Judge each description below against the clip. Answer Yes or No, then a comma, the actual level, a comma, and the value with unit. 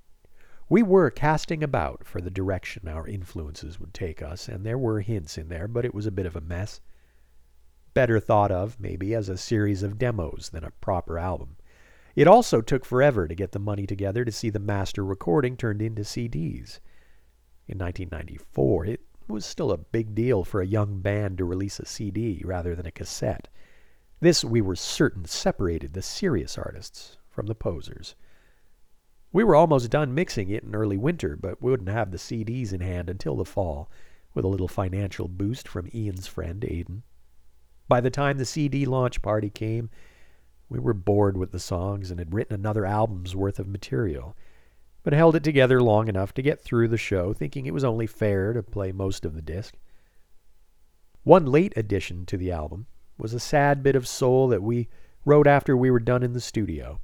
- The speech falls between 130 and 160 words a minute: No, average, 190 wpm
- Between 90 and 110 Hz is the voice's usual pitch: Yes, low, 100 Hz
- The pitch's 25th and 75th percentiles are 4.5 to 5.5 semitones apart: Yes, average, 5.0 semitones